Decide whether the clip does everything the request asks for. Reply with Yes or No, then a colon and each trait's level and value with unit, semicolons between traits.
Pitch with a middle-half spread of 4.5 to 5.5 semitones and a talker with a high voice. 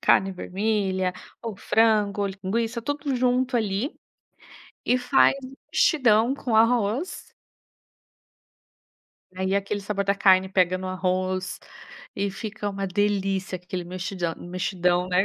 No: average, 3.2 semitones; high, 200 Hz